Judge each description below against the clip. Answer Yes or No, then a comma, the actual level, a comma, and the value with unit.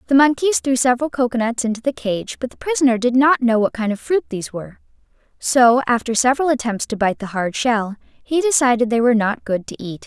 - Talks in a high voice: Yes, high, 240 Hz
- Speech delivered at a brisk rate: Yes, fast, 220 wpm